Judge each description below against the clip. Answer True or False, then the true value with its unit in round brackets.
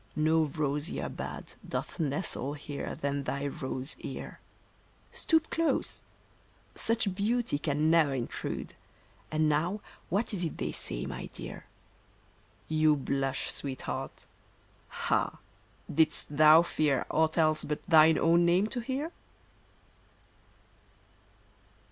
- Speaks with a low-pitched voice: False (155 Hz)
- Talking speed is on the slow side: True (115 wpm)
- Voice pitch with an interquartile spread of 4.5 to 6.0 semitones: False (3.3 semitones)